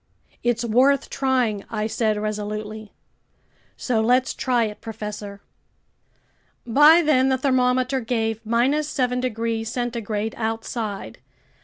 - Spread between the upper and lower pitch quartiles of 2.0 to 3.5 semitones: Yes, average, 2.8 semitones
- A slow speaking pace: Yes, slow, 105 wpm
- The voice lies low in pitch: No, high, 230 Hz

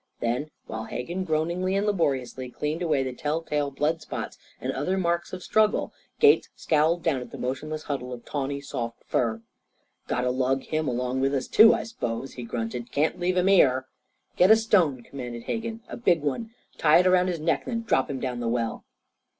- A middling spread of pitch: No, wide, 6.0 semitones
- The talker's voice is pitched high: No, medium, 145 Hz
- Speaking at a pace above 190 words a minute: Yes, average, 200 wpm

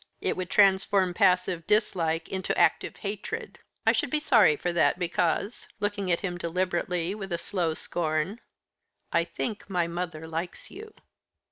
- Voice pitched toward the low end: No, medium, 180 Hz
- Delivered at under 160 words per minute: Yes, average, 150 wpm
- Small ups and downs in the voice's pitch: No, average, 3.1 semitones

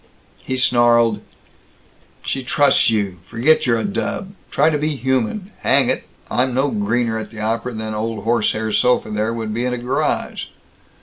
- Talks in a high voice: No, low, 120 Hz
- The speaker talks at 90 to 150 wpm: No, average, 170 wpm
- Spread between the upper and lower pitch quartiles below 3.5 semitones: Yes, average, 3.0 semitones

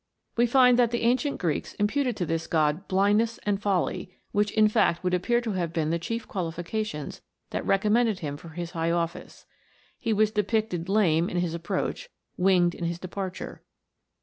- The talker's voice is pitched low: No, high, 190 Hz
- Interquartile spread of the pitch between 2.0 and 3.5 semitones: No, average, 4.4 semitones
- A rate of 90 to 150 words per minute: No, average, 175 wpm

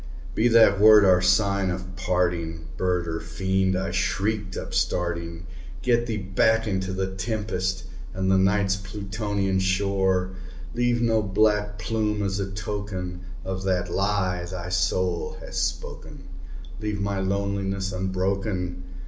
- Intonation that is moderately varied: No, narrow, 1.9 semitones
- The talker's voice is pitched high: No, very low, 95 Hz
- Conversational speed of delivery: No, slow, 130 wpm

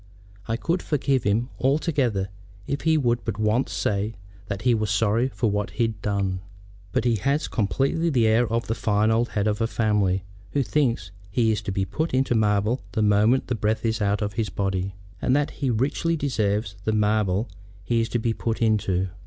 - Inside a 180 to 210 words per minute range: Yes, average, 200 wpm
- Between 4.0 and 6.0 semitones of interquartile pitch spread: No, average, 3.3 semitones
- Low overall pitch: Yes, low, 110 Hz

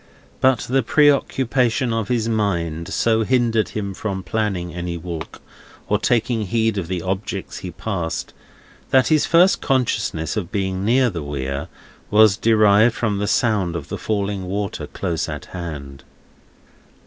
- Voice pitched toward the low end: Yes, low, 105 Hz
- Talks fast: No, average, 150 wpm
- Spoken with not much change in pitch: No, average, 4.6 semitones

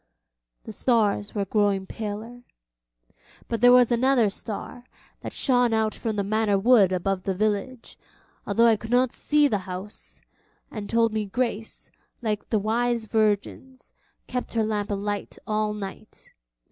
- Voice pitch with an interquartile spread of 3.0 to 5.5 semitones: No, narrow, 2.6 semitones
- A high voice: Yes, high, 215 Hz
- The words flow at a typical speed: Yes, average, 145 wpm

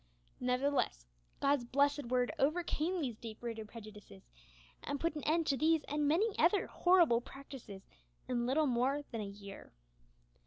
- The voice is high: Yes, very high, 270 Hz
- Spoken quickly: No, average, 150 wpm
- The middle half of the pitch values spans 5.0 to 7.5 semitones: No, average, 4.5 semitones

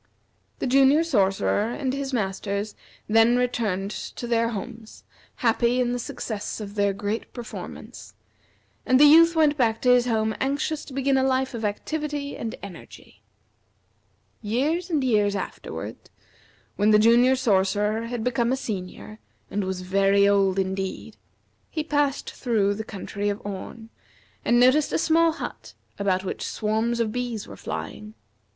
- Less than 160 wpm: Yes, average, 150 wpm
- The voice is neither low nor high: No, high, 230 Hz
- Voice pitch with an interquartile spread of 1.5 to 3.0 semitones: No, average, 4.3 semitones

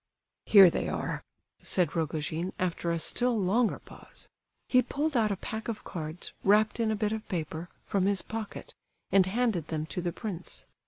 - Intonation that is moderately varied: Yes, average, 4.5 semitones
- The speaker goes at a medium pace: Yes, average, 175 wpm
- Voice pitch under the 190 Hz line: No, high, 195 Hz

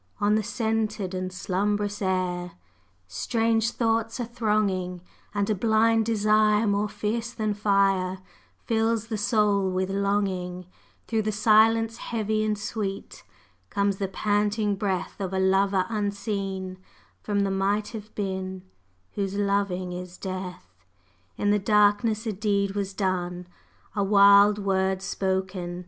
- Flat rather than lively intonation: Yes, narrow, 2.1 semitones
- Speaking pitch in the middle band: No, high, 200 Hz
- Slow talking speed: Yes, slow, 130 wpm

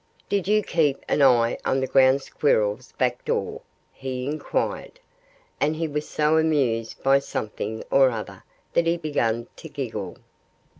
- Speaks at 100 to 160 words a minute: Yes, average, 150 wpm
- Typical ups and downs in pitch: Yes, average, 3.9 semitones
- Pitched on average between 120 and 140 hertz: Yes, low, 135 Hz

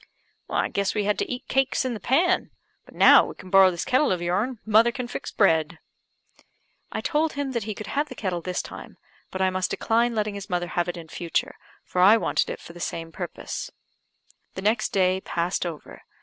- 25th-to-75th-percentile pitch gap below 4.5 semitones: No, average, 5.1 semitones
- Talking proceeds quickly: Yes, fast, 215 wpm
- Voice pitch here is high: Yes, high, 200 Hz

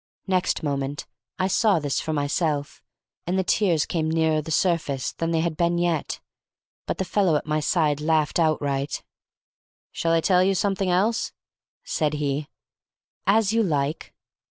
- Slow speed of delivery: No, average, 155 wpm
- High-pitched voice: No, medium, 160 Hz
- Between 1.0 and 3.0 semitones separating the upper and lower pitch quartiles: No, average, 3.6 semitones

